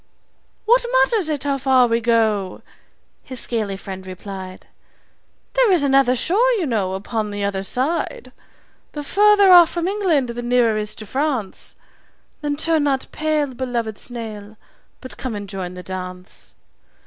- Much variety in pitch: Yes, wide, 7.1 semitones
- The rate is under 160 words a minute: Yes, average, 150 wpm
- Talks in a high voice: Yes, high, 245 Hz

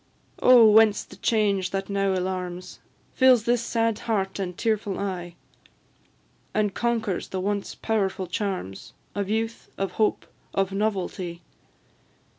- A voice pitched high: Yes, high, 200 Hz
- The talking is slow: Yes, slow, 125 wpm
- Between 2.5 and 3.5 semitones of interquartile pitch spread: Yes, average, 2.8 semitones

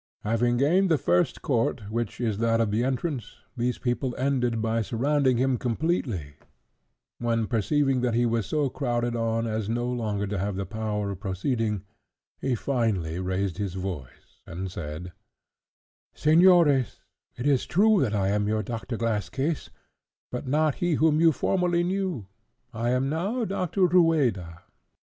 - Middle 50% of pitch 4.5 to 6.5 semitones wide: Yes, wide, 5.6 semitones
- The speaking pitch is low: Yes, low, 120 Hz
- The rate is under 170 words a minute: Yes, average, 155 wpm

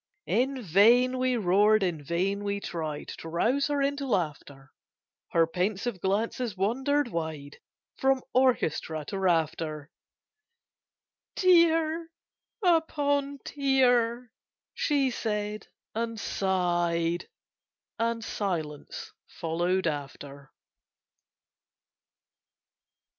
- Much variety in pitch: Yes, wide, 7.3 semitones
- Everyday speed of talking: No, slow, 85 wpm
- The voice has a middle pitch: No, high, 205 Hz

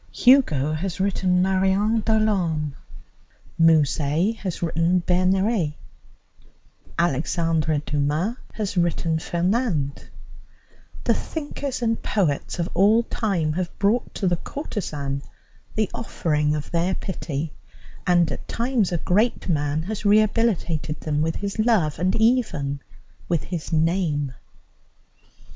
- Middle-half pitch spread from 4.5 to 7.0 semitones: Yes, average, 5.3 semitones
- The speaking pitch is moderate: Yes, medium, 175 Hz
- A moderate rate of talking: No, slow, 115 wpm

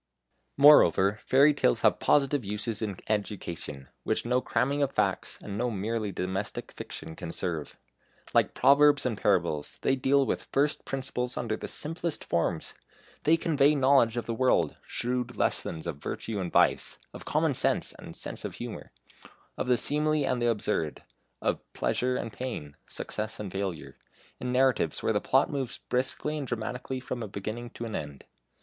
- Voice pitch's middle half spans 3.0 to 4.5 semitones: No, average, 5.1 semitones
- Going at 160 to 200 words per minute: Yes, average, 170 wpm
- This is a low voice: Yes, low, 120 Hz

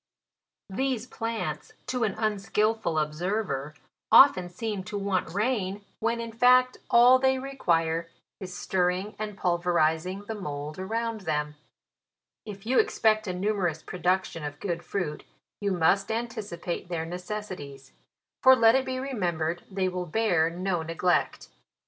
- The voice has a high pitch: Yes, high, 195 Hz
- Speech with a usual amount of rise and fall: Yes, average, 4.6 semitones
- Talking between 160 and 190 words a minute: No, average, 140 wpm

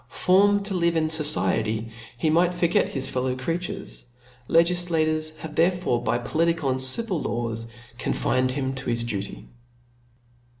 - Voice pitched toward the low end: No, medium, 155 Hz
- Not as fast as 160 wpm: Yes, average, 145 wpm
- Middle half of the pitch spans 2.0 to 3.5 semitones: No, average, 5.0 semitones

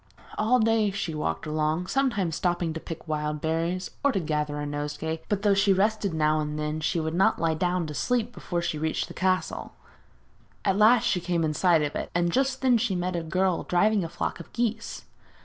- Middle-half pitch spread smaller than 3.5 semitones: No, average, 4.5 semitones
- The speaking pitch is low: No, medium, 175 Hz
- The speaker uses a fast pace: Yes, fast, 220 wpm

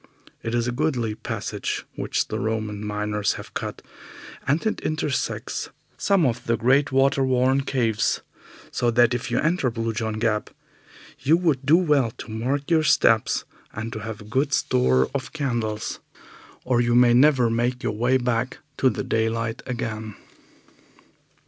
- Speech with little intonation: No, average, 3.4 semitones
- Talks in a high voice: No, low, 120 Hz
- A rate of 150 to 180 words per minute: Yes, average, 160 wpm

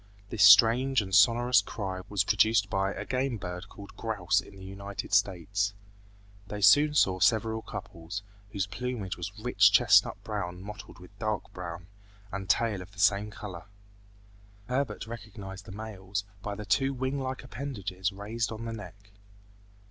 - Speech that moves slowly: No, average, 155 wpm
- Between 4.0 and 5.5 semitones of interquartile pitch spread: No, average, 2.8 semitones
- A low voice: Yes, low, 100 Hz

